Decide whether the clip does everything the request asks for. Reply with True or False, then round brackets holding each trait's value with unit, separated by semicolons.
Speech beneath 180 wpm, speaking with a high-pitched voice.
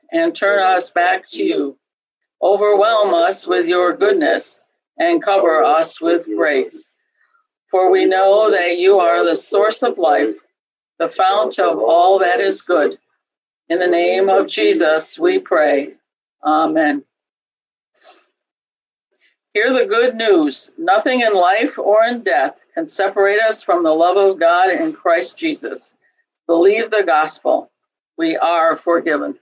True (140 wpm; 210 Hz)